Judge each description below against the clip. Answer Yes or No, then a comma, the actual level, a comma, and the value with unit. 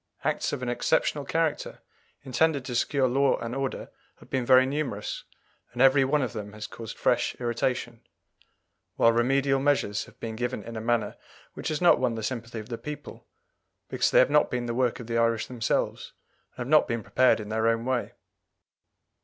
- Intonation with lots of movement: No, average, 2.7 semitones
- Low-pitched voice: Yes, low, 125 Hz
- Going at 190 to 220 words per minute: Yes, average, 195 wpm